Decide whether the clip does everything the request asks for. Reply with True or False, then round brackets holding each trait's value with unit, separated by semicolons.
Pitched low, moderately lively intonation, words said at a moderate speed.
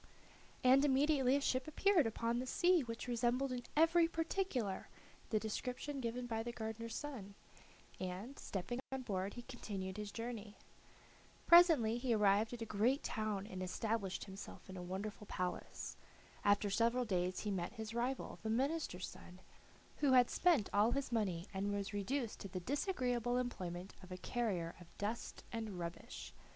False (225 Hz; 4.4 semitones; 165 wpm)